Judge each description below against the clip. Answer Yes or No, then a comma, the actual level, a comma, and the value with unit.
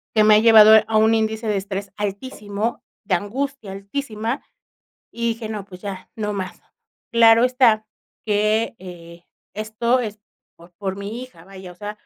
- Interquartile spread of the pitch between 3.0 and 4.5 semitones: No, narrow, 2.4 semitones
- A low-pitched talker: No, high, 215 Hz